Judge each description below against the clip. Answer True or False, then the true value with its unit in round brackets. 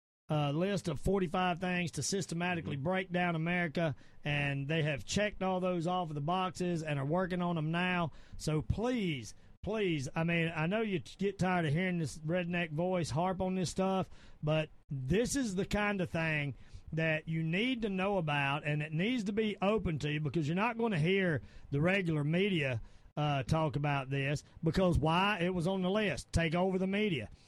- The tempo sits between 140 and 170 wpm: False (200 wpm)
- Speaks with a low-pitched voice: False (170 Hz)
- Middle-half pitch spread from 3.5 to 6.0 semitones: True (3.8 semitones)